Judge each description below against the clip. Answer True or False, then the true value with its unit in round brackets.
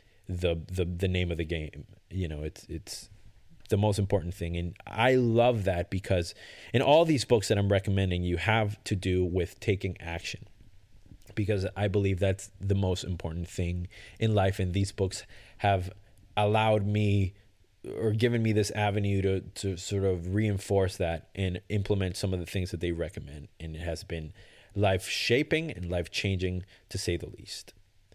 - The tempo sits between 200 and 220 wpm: False (175 wpm)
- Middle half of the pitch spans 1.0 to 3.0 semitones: True (2.5 semitones)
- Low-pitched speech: True (95 Hz)